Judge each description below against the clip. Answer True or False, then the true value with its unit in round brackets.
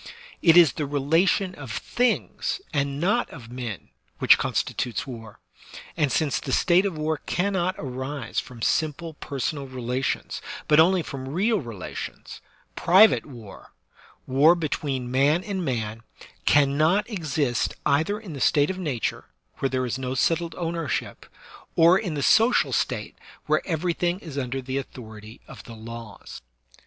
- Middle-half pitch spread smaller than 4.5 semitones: False (5.1 semitones)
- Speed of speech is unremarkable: True (150 wpm)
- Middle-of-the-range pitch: True (145 Hz)